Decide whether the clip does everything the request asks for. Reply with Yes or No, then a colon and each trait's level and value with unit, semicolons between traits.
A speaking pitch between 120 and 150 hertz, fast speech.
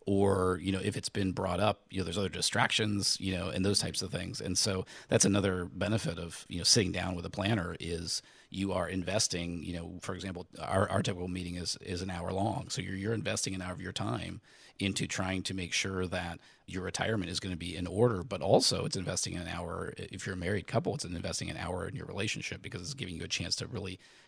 No: very low, 95 Hz; fast, 245 wpm